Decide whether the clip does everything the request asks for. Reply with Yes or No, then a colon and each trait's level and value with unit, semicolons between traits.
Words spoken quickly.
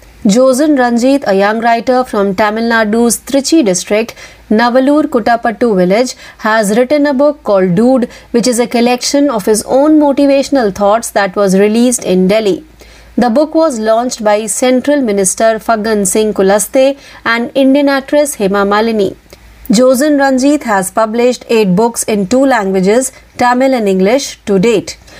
Yes: fast, 150 wpm